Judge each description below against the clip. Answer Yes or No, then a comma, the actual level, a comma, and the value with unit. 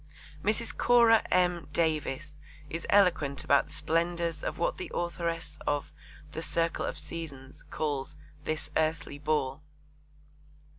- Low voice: No, medium, 160 Hz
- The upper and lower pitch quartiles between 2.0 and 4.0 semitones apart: Yes, narrow, 2.4 semitones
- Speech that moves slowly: Yes, slow, 120 wpm